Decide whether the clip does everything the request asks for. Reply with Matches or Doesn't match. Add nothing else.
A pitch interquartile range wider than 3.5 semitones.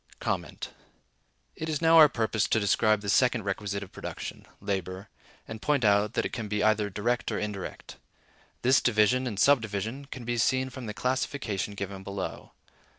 Matches